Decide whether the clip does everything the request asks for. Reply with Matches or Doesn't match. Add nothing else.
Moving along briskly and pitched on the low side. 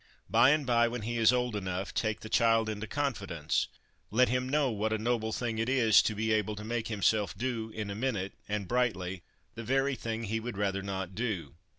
Matches